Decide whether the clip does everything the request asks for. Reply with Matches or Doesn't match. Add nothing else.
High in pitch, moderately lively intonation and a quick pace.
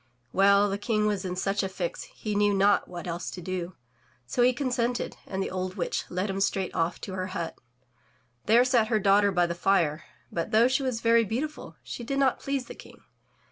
Matches